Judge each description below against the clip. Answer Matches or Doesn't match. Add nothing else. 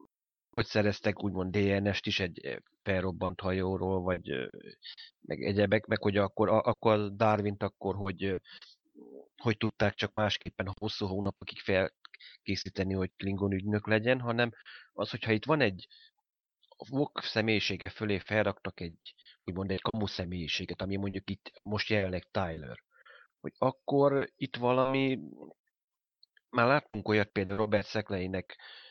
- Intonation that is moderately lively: Doesn't match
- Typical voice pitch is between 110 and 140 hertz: Doesn't match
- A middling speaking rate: Matches